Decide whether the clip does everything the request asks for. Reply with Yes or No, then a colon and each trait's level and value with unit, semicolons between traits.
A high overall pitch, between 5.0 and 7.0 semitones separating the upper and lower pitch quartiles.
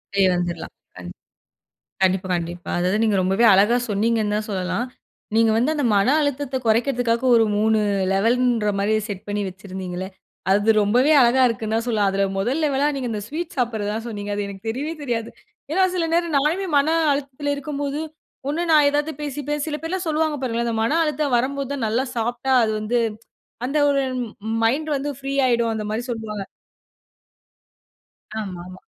Yes: high, 235 Hz; wide, 5.4 semitones